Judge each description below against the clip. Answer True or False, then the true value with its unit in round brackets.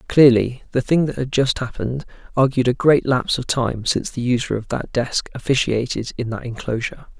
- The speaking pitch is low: True (125 Hz)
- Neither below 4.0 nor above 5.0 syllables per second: False (5.6 syllables/s)